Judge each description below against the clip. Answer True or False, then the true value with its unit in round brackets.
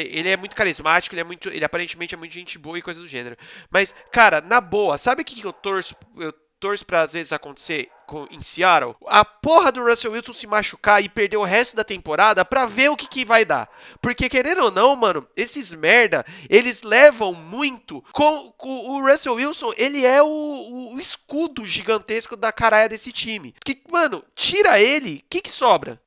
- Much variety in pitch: True (6.0 semitones)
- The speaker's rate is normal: False (205 wpm)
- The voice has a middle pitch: False (225 Hz)